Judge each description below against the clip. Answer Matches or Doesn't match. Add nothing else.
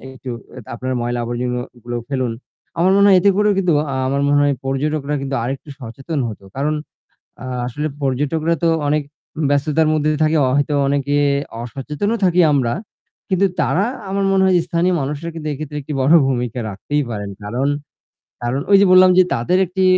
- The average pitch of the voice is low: Doesn't match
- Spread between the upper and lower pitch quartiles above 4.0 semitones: Matches